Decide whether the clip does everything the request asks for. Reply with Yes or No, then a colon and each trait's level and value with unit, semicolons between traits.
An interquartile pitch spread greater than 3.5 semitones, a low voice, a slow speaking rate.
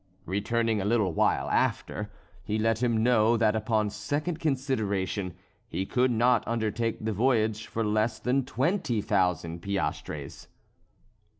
No: average, 2.8 semitones; low, 110 Hz; slow, 130 wpm